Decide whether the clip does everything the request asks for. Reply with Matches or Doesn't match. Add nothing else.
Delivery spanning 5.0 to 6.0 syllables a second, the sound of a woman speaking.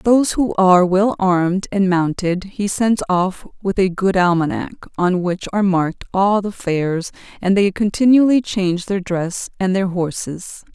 Doesn't match